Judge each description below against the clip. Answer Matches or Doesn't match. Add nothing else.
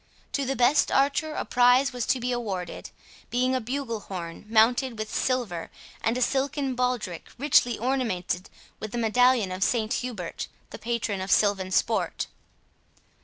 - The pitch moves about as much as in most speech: Matches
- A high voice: Matches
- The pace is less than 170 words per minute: Matches